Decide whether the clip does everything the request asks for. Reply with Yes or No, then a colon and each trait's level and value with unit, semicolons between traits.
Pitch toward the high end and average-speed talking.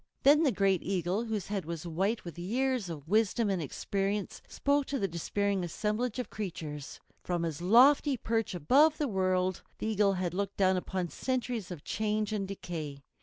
Yes: high, 195 Hz; average, 175 wpm